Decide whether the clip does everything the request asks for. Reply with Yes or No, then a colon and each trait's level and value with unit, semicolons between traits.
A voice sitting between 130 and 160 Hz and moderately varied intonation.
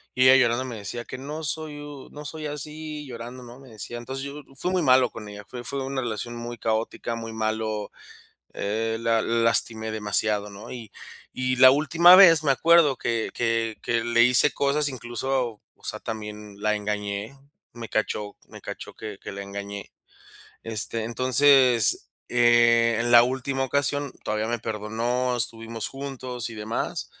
No: low, 120 Hz; average, 3.3 semitones